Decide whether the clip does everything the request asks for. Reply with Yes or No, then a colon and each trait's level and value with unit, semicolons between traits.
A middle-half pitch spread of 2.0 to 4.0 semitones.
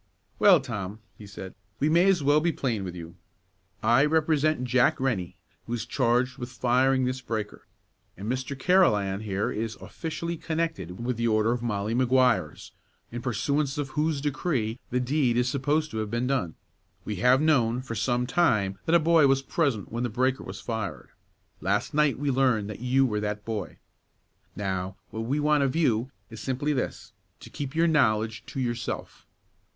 No: average, 4.8 semitones